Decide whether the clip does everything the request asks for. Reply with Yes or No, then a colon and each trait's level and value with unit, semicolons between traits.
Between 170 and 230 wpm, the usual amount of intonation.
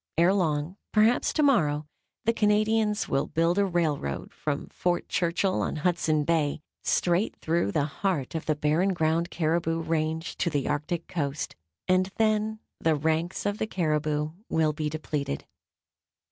No: average, 150 wpm; average, 3.7 semitones